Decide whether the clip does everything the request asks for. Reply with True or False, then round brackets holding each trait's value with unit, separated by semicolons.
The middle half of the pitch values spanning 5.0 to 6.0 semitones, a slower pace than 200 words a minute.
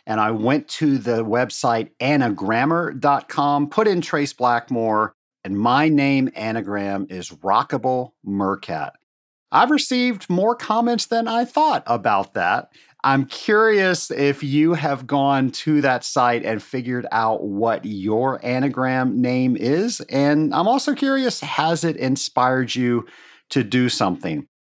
True (5.6 semitones; 135 wpm)